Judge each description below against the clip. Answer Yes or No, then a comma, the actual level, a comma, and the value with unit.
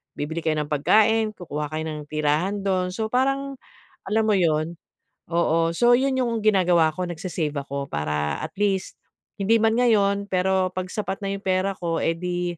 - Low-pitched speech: No, medium, 185 Hz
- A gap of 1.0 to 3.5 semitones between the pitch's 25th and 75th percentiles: No, average, 5.0 semitones